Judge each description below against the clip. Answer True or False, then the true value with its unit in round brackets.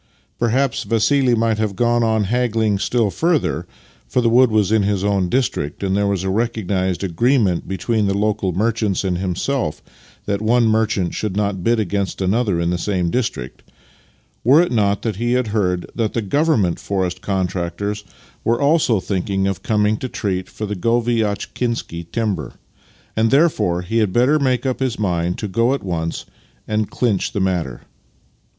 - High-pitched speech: False (105 Hz)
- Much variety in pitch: False (3.8 semitones)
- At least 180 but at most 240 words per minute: False (170 wpm)